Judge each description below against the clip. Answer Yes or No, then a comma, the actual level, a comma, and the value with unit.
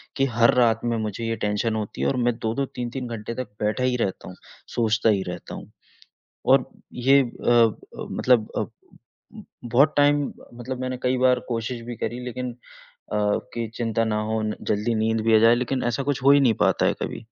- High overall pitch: No, low, 120 Hz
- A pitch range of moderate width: No, narrow, 2.3 semitones